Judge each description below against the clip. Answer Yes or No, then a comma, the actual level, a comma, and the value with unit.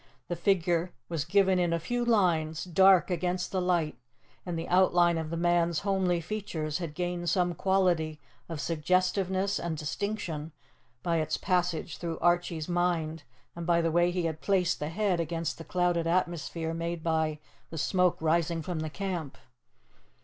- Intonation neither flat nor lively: No, narrow, 1.9 semitones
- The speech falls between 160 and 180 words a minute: Yes, average, 165 wpm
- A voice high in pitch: No, medium, 175 Hz